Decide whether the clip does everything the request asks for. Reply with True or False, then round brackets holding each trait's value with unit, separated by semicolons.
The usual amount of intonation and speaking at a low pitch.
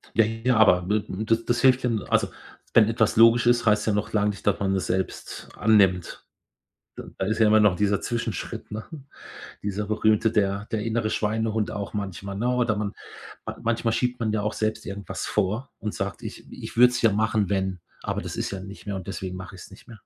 False (2.2 semitones; 105 Hz)